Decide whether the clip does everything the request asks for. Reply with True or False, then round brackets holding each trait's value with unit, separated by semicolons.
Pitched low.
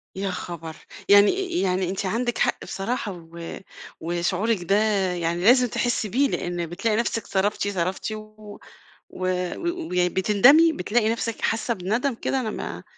False (205 Hz)